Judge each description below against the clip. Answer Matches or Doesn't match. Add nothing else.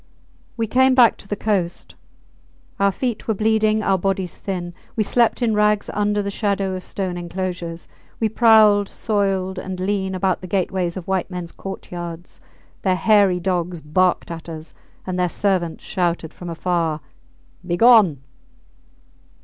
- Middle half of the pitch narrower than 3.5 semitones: Matches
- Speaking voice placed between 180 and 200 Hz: Matches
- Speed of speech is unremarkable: Matches